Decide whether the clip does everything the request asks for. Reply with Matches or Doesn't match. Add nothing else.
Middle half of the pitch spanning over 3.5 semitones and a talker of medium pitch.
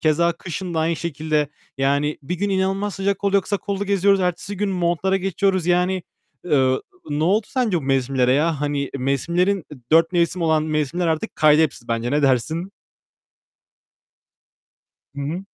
Matches